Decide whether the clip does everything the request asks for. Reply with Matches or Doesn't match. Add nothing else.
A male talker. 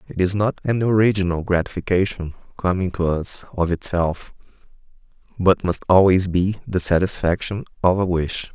Matches